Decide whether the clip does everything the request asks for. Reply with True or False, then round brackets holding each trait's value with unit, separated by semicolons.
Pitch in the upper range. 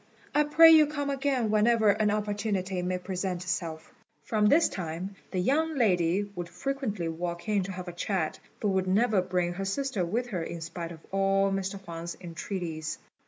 True (195 Hz)